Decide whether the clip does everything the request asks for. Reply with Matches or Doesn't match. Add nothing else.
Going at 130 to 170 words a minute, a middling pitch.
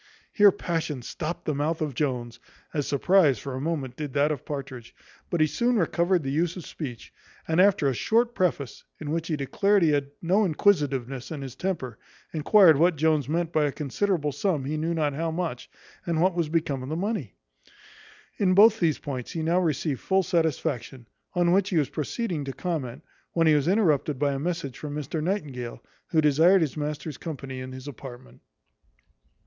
Doesn't match